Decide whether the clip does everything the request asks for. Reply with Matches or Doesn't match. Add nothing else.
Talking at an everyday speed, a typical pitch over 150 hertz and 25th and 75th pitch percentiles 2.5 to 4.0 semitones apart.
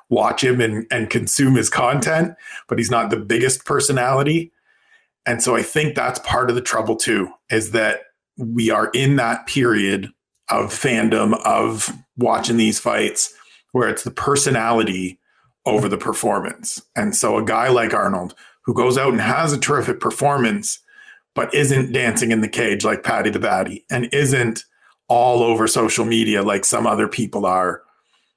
Doesn't match